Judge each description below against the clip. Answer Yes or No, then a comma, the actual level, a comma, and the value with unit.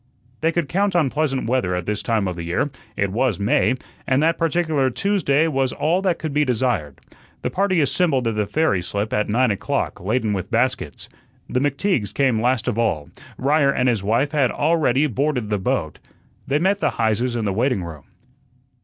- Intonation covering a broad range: Yes, wide, 6.0 semitones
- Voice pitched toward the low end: Yes, low, 130 Hz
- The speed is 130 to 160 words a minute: No, average, 195 wpm